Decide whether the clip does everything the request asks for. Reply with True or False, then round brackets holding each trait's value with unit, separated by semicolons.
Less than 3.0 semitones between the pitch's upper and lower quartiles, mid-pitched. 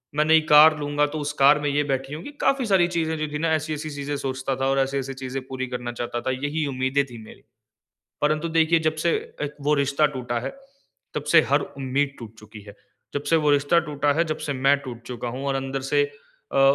True (2.5 semitones; 145 Hz)